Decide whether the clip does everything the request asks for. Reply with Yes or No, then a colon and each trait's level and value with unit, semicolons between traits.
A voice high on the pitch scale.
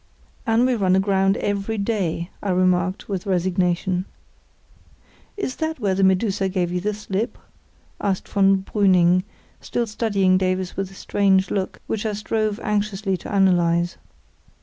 Yes: high, 195 Hz